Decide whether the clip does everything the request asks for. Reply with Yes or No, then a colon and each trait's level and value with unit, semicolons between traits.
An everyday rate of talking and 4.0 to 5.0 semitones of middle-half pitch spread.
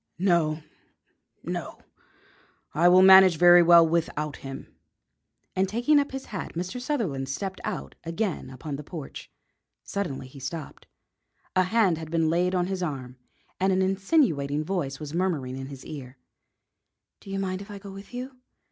Yes: average, 160 wpm; average, 4.5 semitones